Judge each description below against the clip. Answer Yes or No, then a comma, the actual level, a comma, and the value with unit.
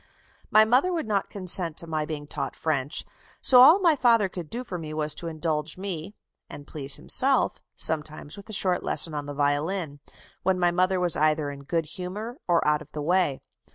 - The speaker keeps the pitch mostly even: No, average, 4.5 semitones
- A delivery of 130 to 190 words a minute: No, average, 200 wpm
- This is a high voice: No, medium, 170 Hz